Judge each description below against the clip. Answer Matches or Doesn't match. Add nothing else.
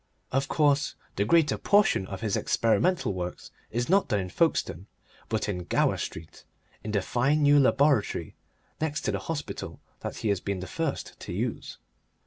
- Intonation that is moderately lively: Doesn't match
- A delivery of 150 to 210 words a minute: Matches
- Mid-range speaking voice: Doesn't match